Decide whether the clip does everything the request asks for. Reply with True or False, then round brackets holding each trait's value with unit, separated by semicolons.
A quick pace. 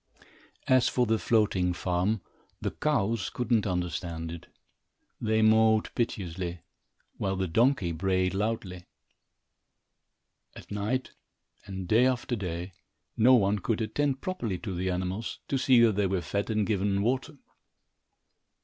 False (135 wpm)